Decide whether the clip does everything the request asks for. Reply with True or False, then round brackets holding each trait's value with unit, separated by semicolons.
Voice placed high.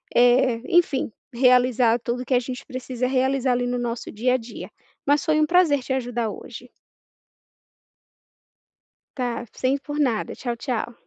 True (250 Hz)